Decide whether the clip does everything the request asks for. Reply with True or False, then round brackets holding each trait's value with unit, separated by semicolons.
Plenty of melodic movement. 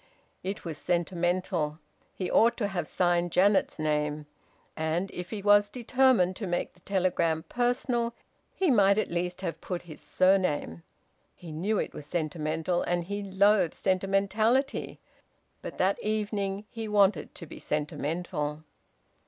False (3.7 semitones)